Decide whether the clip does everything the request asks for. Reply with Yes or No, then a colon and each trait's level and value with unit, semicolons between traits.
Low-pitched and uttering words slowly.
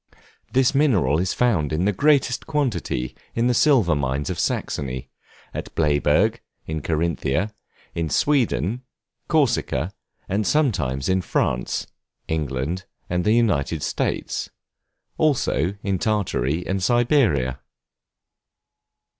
Yes: very low, 90 Hz; slow, 110 wpm